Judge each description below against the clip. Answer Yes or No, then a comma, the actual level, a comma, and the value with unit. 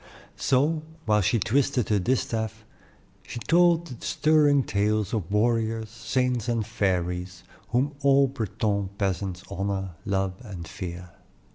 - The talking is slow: Yes, slow, 125 wpm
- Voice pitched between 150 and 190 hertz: No, low, 110 Hz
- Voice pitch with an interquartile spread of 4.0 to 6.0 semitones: Yes, average, 4.8 semitones